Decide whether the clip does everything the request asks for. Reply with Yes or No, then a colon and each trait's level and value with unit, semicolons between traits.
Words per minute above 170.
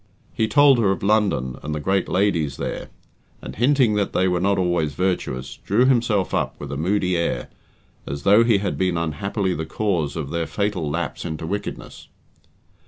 Yes: average, 180 wpm